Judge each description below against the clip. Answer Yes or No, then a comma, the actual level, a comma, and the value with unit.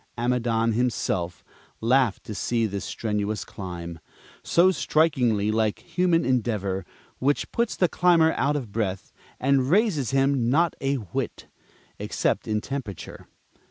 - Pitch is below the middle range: Yes, low, 120 Hz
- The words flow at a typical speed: No, slow, 125 wpm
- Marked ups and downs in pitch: No, average, 5.0 semitones